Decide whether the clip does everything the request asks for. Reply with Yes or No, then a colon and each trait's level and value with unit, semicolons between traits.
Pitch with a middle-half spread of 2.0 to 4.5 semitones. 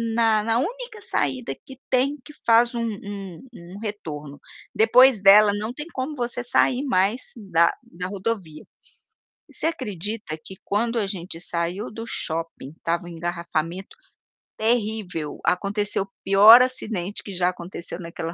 No: average, 5.1 semitones